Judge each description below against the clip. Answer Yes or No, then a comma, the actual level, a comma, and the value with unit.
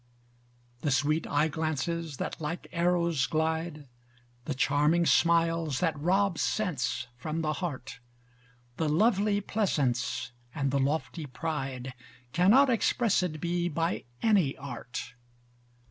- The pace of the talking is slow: Yes, slow, 115 wpm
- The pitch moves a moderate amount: Yes, average, 3.5 semitones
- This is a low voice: No, medium, 160 Hz